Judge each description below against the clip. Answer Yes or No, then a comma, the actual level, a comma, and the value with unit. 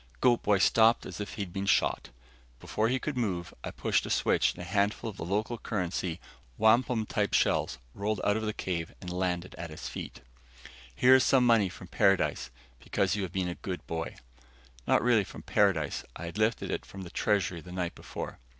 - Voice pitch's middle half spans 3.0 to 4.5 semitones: Yes, average, 3.8 semitones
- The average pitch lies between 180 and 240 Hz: No, low, 100 Hz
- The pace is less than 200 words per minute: No, fast, 205 wpm